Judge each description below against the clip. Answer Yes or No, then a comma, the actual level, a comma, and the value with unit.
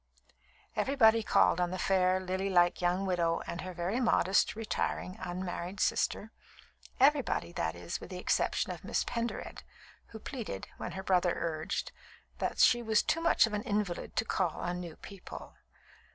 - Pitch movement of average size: Yes, average, 3.8 semitones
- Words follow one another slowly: No, average, 160 wpm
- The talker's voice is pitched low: No, medium, 185 Hz